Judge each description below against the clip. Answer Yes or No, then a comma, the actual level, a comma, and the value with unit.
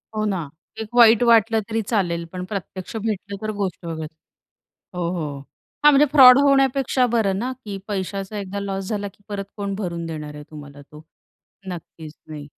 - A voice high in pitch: Yes, high, 200 Hz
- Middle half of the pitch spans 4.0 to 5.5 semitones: Yes, average, 4.7 semitones